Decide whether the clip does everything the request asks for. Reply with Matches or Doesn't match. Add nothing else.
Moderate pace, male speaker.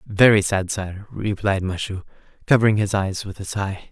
Matches